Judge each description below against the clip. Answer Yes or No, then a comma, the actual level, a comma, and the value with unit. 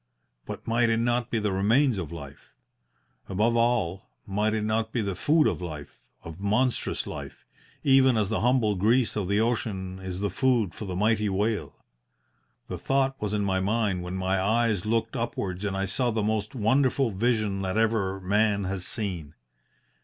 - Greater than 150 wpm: Yes, average, 180 wpm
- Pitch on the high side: No, low, 105 Hz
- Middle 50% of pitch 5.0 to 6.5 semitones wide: No, average, 3.4 semitones